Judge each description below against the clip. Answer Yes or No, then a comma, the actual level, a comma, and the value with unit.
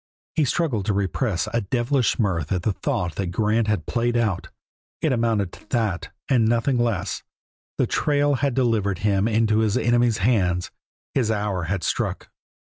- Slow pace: No, average, 165 wpm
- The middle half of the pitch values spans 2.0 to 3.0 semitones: No, average, 3.6 semitones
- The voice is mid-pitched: No, low, 110 Hz